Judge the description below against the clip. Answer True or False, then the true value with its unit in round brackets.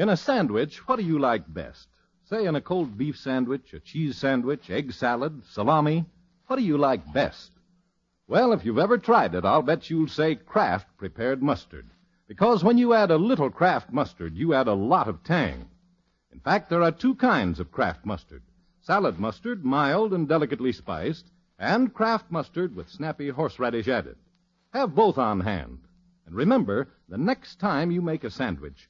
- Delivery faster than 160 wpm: True (180 wpm)